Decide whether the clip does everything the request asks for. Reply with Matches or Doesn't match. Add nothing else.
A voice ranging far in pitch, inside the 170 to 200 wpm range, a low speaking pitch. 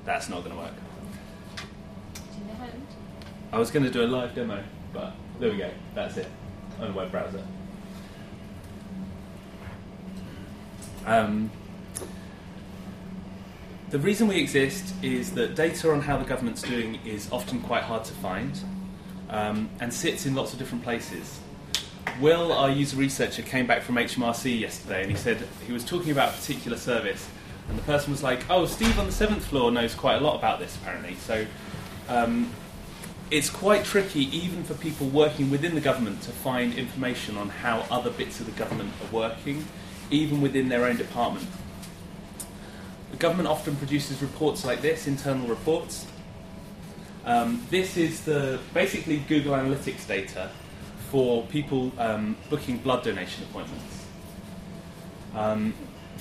Doesn't match